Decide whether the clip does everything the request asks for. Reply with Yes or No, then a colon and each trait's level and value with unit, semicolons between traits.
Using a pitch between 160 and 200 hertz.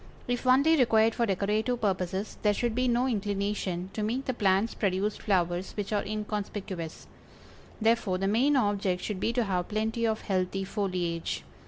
No: high, 210 Hz